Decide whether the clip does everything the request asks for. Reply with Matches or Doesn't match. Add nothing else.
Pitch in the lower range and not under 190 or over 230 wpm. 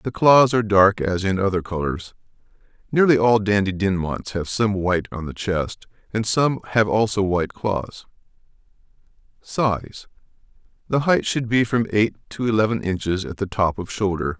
Doesn't match